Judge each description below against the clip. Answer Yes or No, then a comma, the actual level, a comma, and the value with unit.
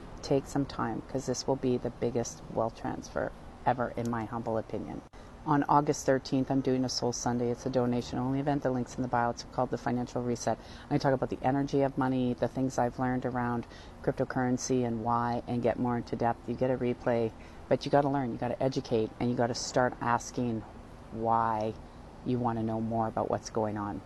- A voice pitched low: Yes, low, 120 Hz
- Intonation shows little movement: Yes, narrow, 2.0 semitones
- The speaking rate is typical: No, fast, 220 wpm